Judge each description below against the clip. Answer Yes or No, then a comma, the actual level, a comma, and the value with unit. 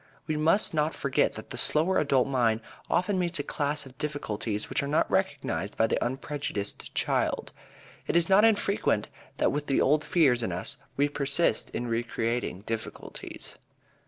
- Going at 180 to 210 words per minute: No, average, 165 wpm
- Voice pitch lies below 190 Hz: Yes, medium, 140 Hz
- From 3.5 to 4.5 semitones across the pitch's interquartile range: No, average, 5.0 semitones